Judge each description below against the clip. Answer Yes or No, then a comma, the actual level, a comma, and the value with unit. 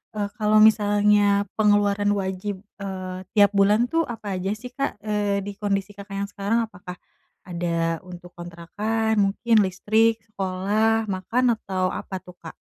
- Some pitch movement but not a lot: No, narrow, 2.3 semitones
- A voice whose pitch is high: Yes, high, 205 Hz